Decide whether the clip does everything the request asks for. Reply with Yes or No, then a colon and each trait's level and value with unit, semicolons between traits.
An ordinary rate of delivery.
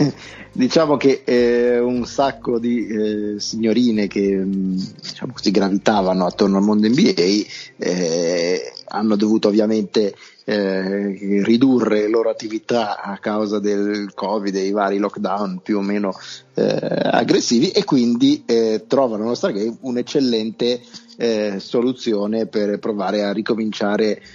Yes: average, 130 wpm